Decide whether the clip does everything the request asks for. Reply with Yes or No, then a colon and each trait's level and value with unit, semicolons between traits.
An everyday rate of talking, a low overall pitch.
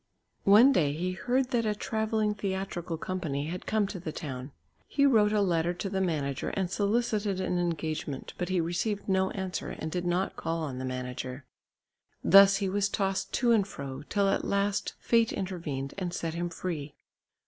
No: average, 180 wpm; medium, 185 Hz